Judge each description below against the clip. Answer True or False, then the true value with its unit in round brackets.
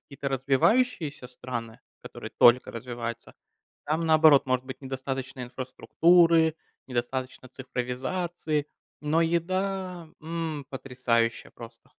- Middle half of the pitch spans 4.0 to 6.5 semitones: True (4.4 semitones)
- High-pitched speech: False (135 Hz)